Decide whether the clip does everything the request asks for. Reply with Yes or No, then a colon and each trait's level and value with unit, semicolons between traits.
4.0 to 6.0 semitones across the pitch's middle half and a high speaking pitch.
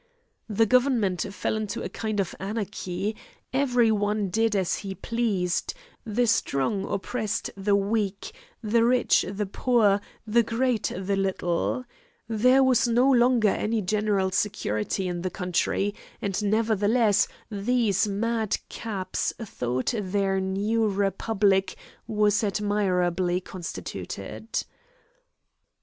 No: average, 2.9 semitones; high, 205 Hz